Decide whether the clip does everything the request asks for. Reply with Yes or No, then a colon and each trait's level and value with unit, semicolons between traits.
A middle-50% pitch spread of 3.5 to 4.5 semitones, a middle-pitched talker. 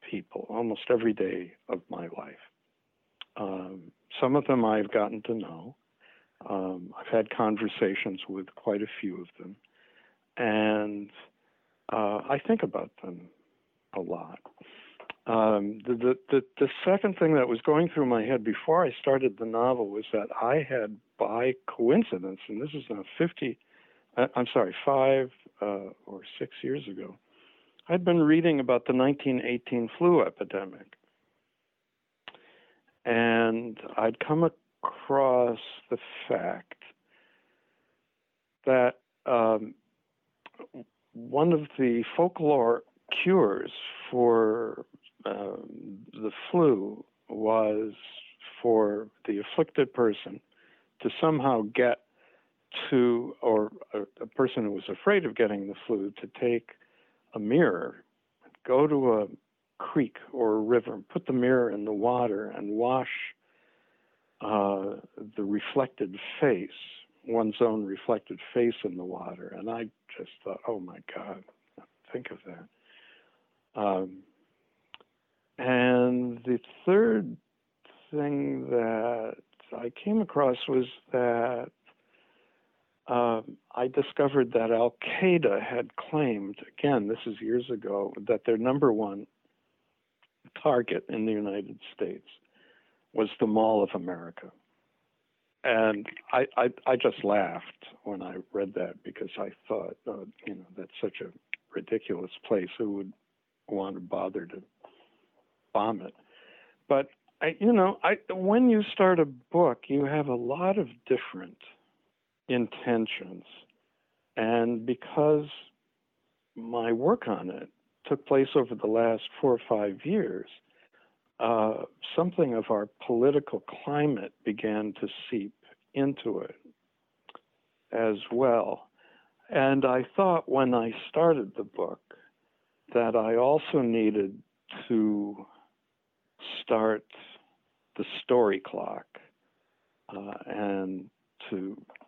No: average, 4.2 semitones; low, 120 Hz